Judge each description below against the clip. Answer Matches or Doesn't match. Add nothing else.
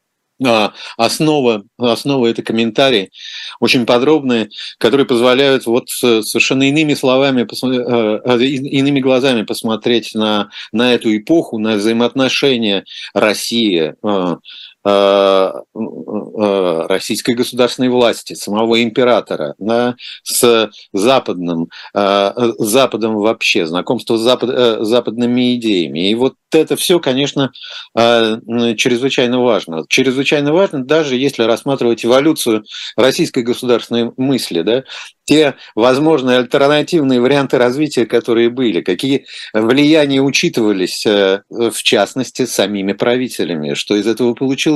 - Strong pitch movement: Doesn't match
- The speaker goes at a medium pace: Doesn't match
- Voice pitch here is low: Matches